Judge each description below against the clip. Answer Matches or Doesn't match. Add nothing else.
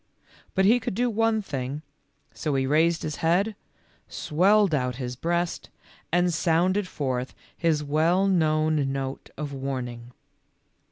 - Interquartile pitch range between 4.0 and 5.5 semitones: Matches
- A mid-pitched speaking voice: Matches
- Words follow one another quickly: Doesn't match